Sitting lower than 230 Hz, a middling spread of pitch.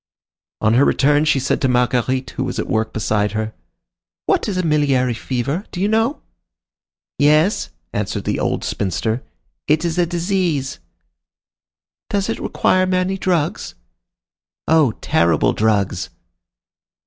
No: medium, 140 Hz; wide, 7.9 semitones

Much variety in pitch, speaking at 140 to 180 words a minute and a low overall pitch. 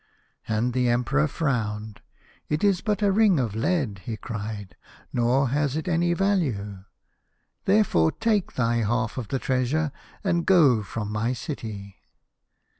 Yes: wide, 7.5 semitones; average, 155 wpm; low, 125 Hz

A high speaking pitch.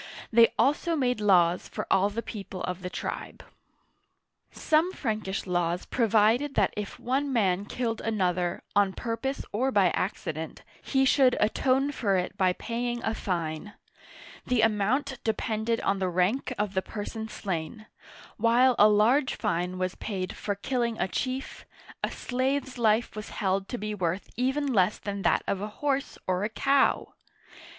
Yes: high, 215 Hz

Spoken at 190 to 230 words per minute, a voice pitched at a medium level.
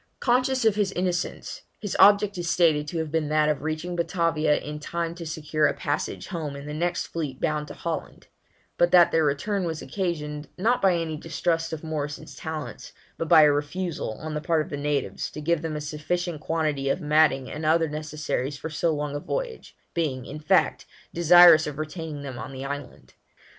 Yes: average, 200 wpm; medium, 155 Hz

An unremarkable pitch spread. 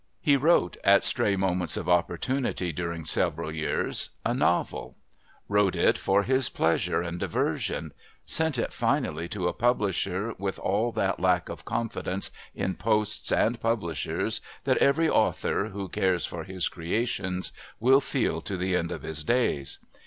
Yes: average, 4.9 semitones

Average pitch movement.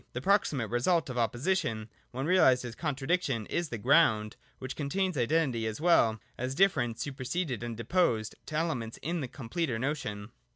No: wide, 6.1 semitones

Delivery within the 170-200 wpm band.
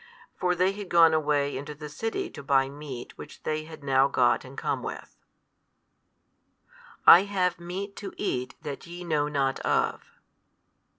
No: average, 160 wpm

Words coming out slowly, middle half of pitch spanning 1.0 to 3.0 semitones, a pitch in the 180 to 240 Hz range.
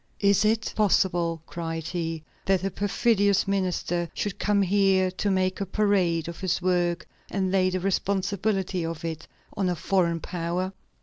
No: average, 160 wpm; narrow, 2.5 semitones; medium, 185 Hz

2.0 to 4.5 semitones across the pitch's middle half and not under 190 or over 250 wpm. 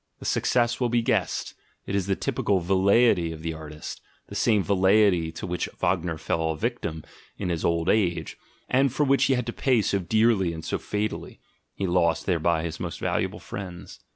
No: average, 4.9 semitones; average, 195 wpm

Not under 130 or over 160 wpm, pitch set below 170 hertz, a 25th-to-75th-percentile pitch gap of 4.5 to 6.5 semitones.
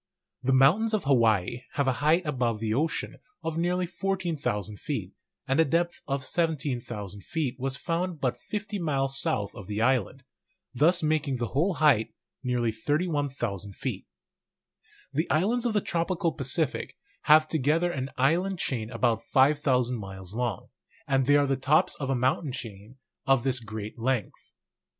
Yes: average, 155 wpm; low, 135 Hz; average, 5.2 semitones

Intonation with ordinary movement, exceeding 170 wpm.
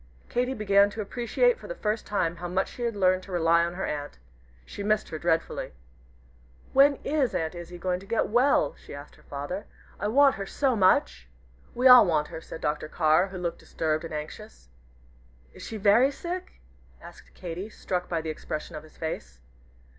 No: wide, 5.7 semitones; average, 190 wpm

